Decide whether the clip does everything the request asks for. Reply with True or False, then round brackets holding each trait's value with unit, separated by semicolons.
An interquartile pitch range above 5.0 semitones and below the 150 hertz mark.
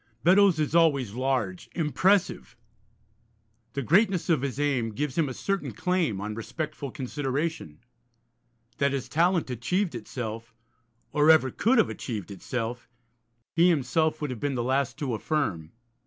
True (5.4 semitones; 140 Hz)